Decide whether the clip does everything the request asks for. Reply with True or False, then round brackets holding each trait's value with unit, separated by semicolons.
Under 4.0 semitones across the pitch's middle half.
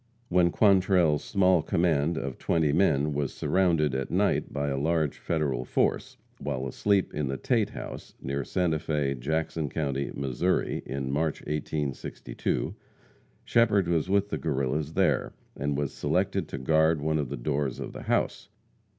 True (3.5 semitones)